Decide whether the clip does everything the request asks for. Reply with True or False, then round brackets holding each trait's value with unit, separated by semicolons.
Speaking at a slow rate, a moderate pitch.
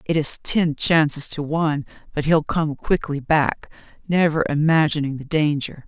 False (155 wpm; 150 Hz)